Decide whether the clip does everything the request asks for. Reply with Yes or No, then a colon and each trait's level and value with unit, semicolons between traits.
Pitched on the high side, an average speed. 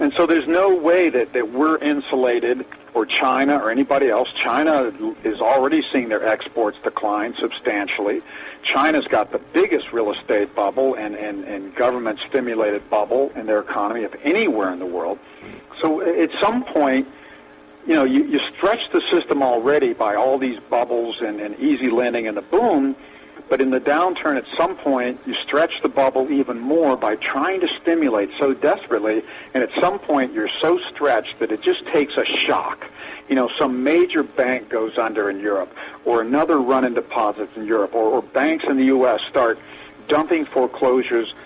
No: low, 135 Hz; average, 180 wpm